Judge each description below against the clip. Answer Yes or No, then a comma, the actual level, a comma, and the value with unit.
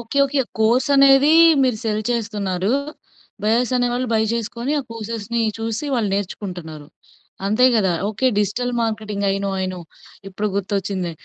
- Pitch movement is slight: No, average, 3.2 semitones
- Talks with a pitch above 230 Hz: No, high, 220 Hz